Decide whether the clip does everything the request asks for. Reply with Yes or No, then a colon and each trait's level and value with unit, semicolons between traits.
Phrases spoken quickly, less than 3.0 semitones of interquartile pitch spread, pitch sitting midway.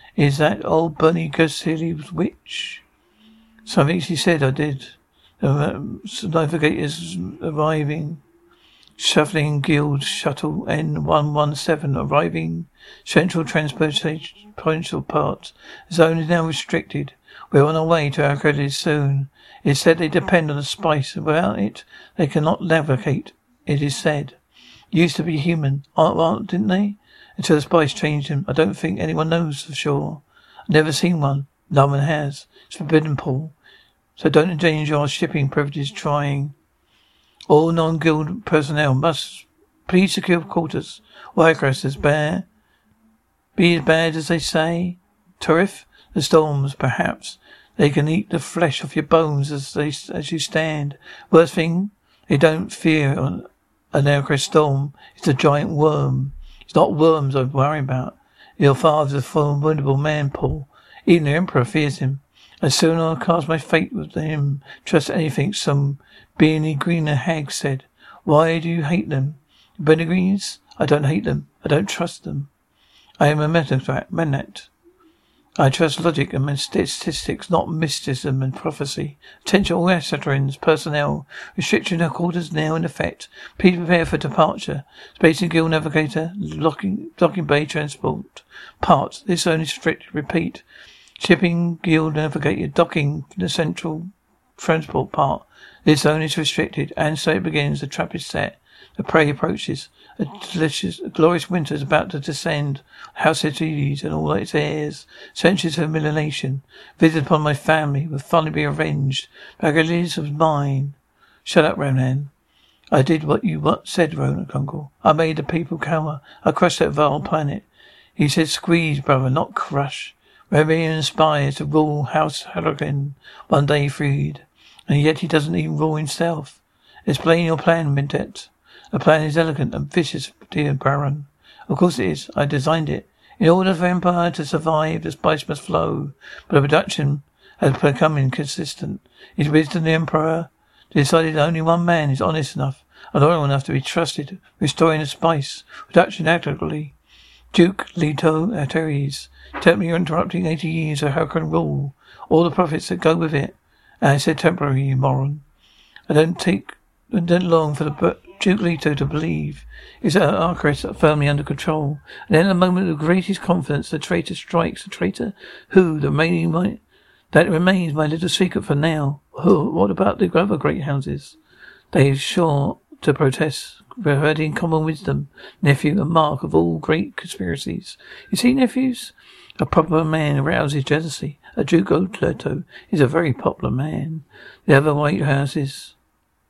No: average, 160 wpm; narrow, 2.6 semitones; medium, 155 Hz